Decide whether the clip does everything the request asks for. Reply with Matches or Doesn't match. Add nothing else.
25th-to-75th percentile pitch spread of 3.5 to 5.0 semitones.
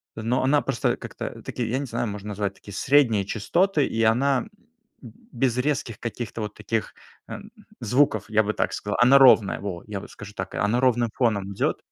Matches